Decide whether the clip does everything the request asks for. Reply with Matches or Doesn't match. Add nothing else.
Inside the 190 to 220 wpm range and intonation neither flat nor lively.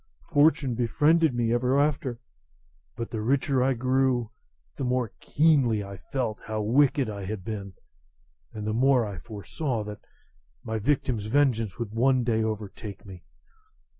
Doesn't match